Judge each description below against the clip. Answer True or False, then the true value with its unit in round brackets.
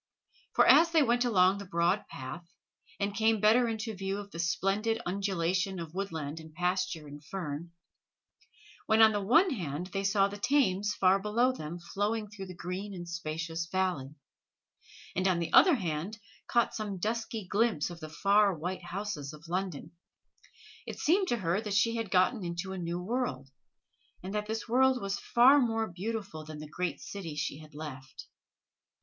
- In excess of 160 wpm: True (175 wpm)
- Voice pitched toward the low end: False (195 Hz)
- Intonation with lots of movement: False (4.3 semitones)